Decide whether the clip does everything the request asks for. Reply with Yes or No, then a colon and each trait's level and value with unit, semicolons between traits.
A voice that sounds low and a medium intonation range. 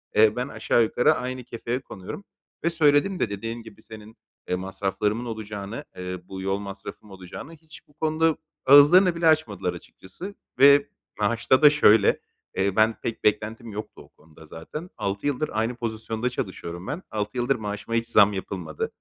No: low, 110 Hz; wide, 5.9 semitones